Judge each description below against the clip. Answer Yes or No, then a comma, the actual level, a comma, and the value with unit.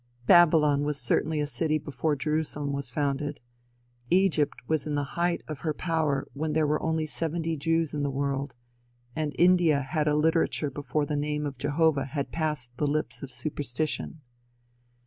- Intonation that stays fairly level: Yes, narrow, 2.0 semitones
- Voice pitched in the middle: Yes, medium, 150 Hz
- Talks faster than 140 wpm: Yes, average, 165 wpm